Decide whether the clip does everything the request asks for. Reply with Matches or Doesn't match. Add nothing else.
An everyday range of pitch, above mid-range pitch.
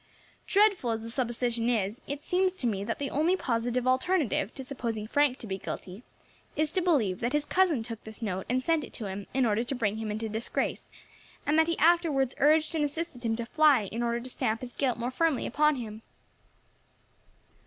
Matches